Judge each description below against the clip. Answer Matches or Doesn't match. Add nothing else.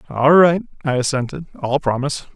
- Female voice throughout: Doesn't match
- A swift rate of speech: Doesn't match